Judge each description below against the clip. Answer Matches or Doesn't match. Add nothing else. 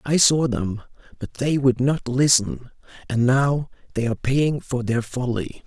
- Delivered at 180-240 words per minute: Doesn't match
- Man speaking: Matches